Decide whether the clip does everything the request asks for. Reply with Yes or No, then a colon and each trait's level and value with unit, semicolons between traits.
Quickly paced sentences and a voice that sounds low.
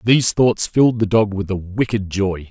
Yes: fast, 215 wpm; low, 105 Hz